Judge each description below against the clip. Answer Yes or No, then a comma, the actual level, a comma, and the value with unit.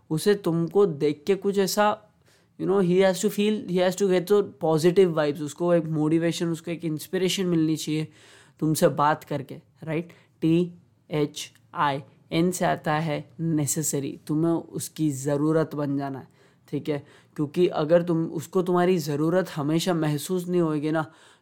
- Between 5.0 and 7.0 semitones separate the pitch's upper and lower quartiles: No, average, 3.0 semitones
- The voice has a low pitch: No, medium, 160 Hz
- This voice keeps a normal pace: Yes, average, 165 wpm